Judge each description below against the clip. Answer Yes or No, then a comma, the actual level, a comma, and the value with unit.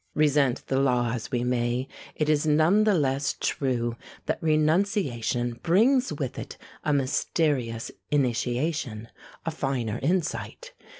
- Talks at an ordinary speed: No, slow, 125 wpm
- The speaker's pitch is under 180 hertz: Yes, medium, 140 Hz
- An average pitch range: Yes, average, 4.5 semitones